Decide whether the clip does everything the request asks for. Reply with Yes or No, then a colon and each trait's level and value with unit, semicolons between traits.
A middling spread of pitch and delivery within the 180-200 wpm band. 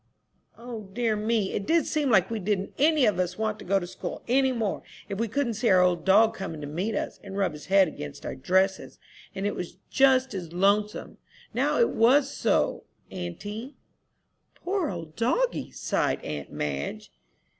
Yes: average, 4.7 semitones; average, 185 wpm